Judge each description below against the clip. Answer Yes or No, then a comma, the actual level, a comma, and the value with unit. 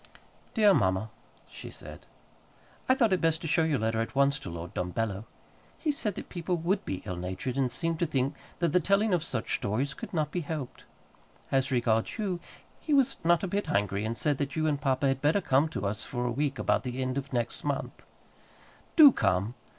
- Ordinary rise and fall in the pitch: No, wide, 7.1 semitones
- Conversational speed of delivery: No, fast, 210 wpm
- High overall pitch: No, medium, 140 Hz